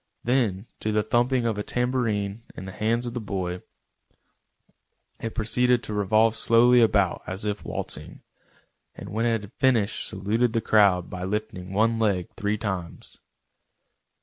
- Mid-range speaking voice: No, low, 110 Hz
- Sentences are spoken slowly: No, average, 150 wpm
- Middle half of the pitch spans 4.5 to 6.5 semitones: No, average, 2.9 semitones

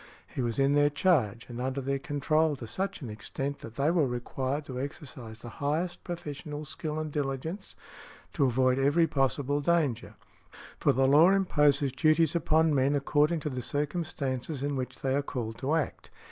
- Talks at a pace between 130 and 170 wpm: No, average, 180 wpm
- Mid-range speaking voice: Yes, medium, 145 Hz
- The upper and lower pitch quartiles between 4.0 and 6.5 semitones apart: No, average, 3.0 semitones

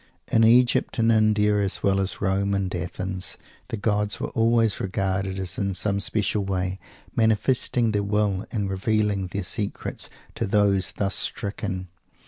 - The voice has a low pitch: Yes, low, 100 Hz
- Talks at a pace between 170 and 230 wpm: No, average, 155 wpm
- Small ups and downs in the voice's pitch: Yes, narrow, 1.9 semitones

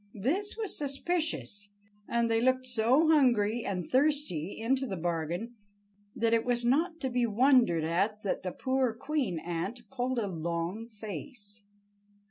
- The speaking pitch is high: Yes, high, 235 Hz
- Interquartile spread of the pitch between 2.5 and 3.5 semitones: No, average, 5.0 semitones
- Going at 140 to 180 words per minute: Yes, average, 145 wpm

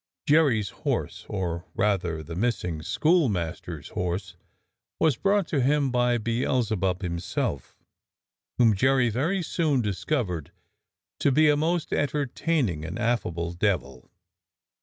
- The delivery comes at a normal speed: No, slow, 115 wpm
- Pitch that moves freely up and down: Yes, wide, 8.4 semitones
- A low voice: Yes, low, 115 Hz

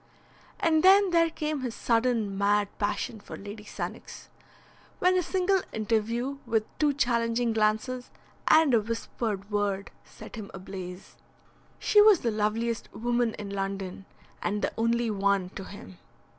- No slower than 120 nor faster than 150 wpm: Yes, average, 145 wpm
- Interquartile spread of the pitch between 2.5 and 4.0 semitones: Yes, average, 3.7 semitones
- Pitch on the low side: No, high, 225 Hz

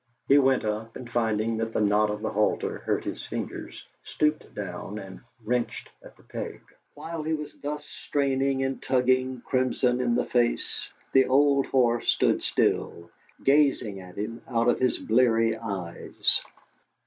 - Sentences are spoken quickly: No, average, 160 wpm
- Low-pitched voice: Yes, low, 120 Hz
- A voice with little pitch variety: No, average, 3.6 semitones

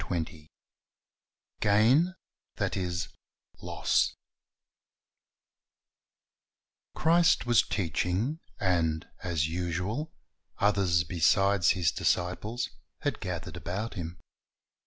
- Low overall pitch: Yes, very low, 90 Hz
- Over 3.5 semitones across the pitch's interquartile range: Yes, average, 4.3 semitones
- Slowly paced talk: Yes, slow, 75 wpm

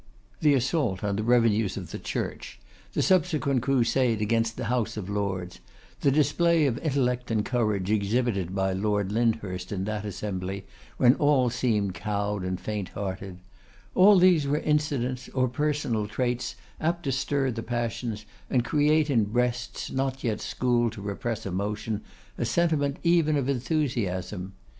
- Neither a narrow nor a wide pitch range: Yes, average, 4.9 semitones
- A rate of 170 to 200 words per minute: No, average, 150 wpm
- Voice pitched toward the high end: No, low, 120 Hz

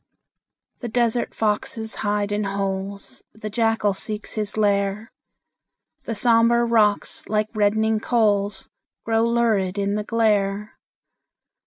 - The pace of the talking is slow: Yes, slow, 115 wpm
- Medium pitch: No, high, 215 Hz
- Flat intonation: Yes, narrow, 2.0 semitones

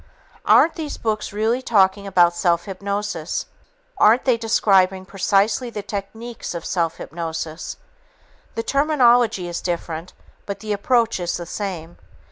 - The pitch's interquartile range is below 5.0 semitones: Yes, average, 4.6 semitones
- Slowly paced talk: Yes, slow, 130 wpm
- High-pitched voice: Yes, high, 200 Hz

